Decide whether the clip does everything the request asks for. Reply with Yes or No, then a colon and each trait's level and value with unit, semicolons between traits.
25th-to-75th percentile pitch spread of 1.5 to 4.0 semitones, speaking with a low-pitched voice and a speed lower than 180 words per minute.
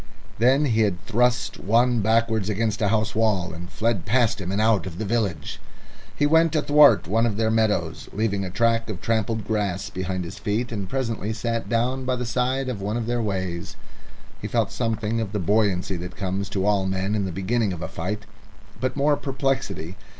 No: average, 3.3 semitones; low, 110 Hz; average, 195 wpm